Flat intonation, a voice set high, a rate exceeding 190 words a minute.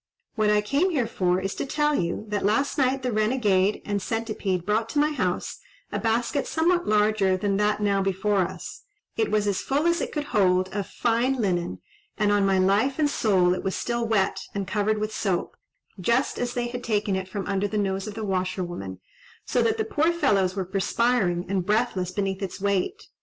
No: average, 4.0 semitones; high, 210 Hz; fast, 205 wpm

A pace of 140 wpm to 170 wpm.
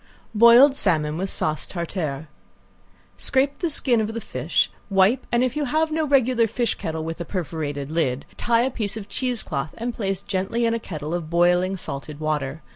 No: average, 190 wpm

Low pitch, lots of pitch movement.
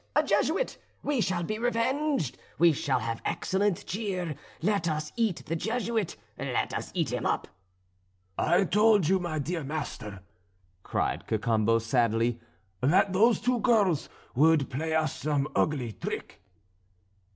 No: medium, 165 Hz; wide, 7.2 semitones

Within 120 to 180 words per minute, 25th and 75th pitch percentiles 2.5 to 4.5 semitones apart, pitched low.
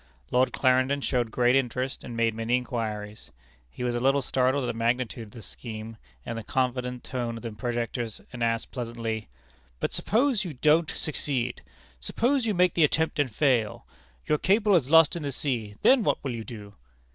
No: average, 190 wpm; average, 3.7 semitones; low, 125 Hz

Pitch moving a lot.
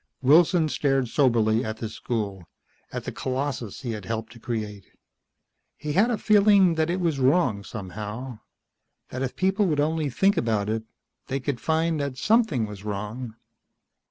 Yes: wide, 6.4 semitones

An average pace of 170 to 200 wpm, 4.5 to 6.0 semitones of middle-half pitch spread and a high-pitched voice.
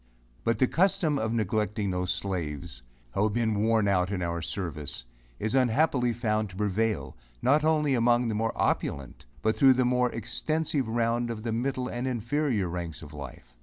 No: average, 175 wpm; average, 5.1 semitones; low, 110 Hz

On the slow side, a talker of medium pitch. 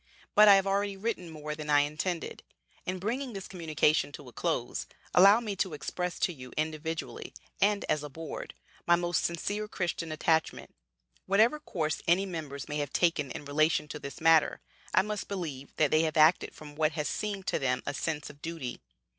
No: average, 190 wpm; medium, 165 Hz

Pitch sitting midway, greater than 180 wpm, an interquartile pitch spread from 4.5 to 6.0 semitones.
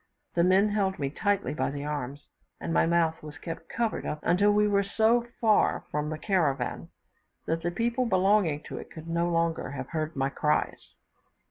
Yes: medium, 170 Hz; average, 190 wpm; average, 5.0 semitones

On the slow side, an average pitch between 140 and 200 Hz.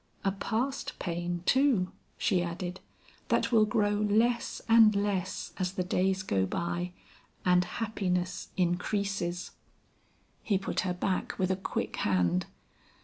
Yes: slow, 130 wpm; medium, 185 Hz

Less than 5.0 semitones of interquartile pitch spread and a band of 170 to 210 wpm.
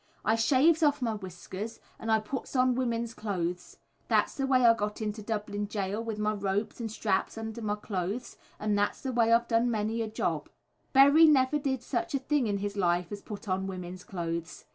Yes: average, 3.3 semitones; fast, 205 wpm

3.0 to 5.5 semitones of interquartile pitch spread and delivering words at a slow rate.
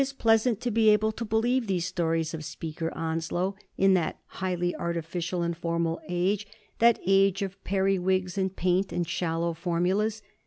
No: average, 3.4 semitones; average, 165 wpm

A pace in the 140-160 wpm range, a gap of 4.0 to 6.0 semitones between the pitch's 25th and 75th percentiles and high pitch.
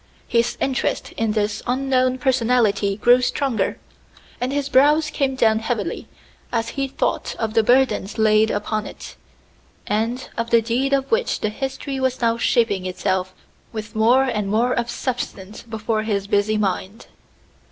No: average, 150 wpm; average, 3.3 semitones; high, 230 Hz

